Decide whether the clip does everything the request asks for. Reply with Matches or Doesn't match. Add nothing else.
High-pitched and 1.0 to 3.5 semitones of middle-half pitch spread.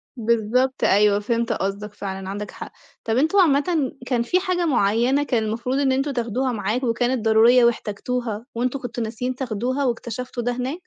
Matches